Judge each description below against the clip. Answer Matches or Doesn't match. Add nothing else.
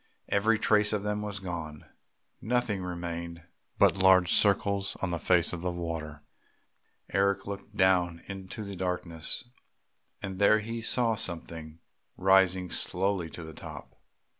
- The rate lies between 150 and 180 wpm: Doesn't match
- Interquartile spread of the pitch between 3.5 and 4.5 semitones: Doesn't match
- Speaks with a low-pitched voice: Matches